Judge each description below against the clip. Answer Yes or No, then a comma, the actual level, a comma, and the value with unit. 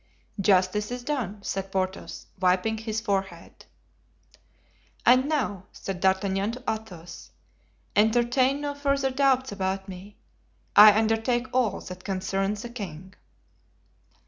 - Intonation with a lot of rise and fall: No, average, 4.4 semitones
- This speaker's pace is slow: Yes, slow, 115 wpm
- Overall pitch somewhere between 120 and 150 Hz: No, high, 210 Hz